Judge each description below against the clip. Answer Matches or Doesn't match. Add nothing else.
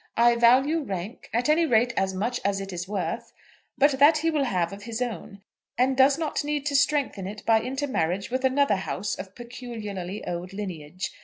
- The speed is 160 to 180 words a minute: Doesn't match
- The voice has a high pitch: Matches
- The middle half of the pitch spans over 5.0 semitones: Matches